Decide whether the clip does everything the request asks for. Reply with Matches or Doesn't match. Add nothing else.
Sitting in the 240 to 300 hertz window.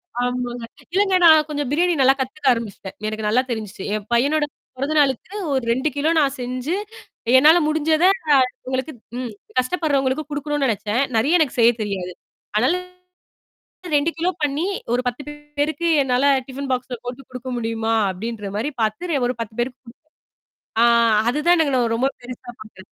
Matches